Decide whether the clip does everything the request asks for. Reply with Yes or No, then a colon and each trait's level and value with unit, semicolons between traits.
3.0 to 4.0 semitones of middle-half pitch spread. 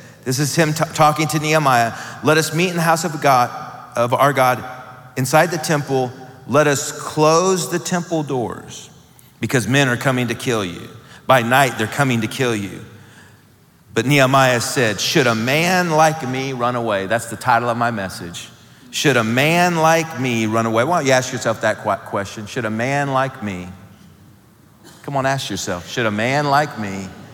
No: average, 4.5 semitones